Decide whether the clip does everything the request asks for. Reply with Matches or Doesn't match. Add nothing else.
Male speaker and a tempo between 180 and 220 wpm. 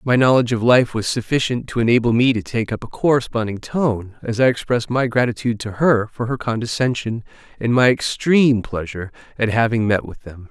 Matches